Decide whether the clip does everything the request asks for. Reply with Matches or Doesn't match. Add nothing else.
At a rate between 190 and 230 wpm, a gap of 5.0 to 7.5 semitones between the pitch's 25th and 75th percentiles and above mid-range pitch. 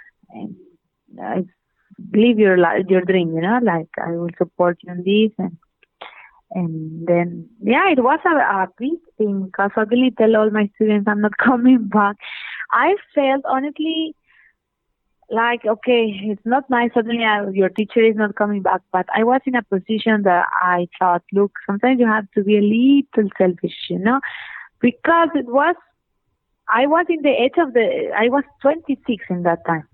Doesn't match